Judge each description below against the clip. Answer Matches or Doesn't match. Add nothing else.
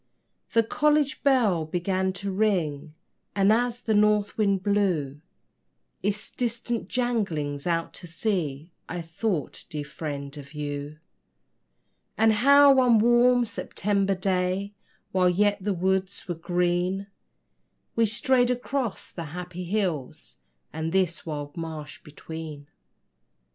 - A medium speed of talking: Doesn't match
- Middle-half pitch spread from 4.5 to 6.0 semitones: Matches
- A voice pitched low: Doesn't match